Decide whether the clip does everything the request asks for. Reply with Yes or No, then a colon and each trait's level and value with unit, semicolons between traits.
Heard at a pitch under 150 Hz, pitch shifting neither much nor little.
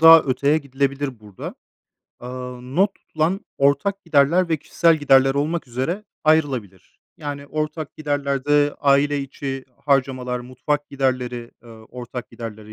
Yes: medium, 140 Hz; average, 3.0 semitones